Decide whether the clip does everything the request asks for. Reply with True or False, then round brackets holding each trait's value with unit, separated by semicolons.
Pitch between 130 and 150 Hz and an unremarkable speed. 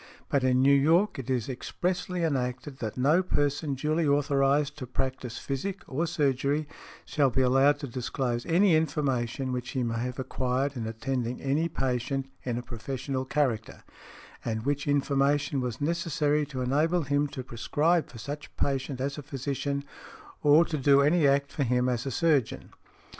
True (140 Hz; 170 wpm)